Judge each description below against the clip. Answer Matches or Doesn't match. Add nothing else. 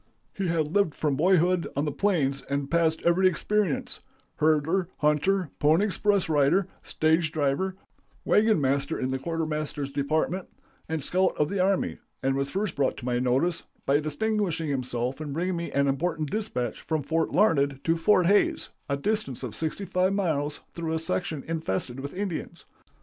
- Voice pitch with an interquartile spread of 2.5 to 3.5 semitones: Doesn't match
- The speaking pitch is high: Doesn't match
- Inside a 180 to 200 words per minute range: Doesn't match